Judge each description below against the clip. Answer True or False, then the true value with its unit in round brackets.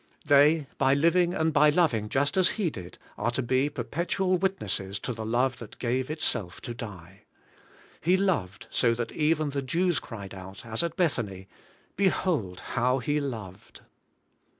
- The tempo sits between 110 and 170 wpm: True (165 wpm)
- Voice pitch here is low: True (130 Hz)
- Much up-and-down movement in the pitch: True (6.5 semitones)